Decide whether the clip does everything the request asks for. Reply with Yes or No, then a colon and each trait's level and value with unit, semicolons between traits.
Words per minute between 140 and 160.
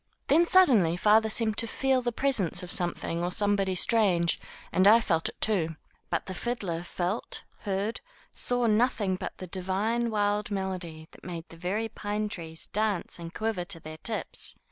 No: average, 175 wpm